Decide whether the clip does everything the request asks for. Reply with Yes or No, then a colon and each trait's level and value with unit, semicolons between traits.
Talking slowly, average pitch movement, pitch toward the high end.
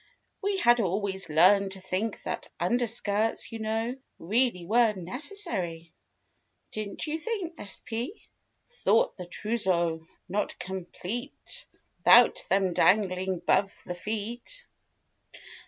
Yes: slow, 105 wpm; average, 4.7 semitones; high, 210 Hz